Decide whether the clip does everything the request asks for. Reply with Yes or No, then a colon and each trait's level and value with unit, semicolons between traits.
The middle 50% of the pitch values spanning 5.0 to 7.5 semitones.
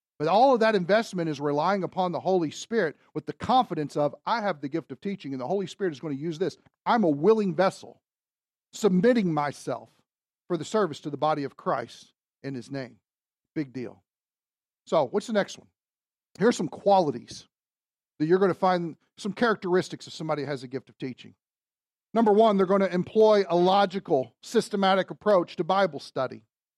Yes: average, 5.3 semitones